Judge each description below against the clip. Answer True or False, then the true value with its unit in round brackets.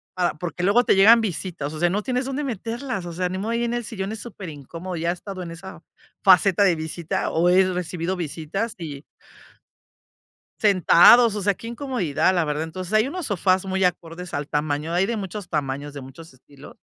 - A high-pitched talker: False (180 Hz)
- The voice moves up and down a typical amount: True (4.1 semitones)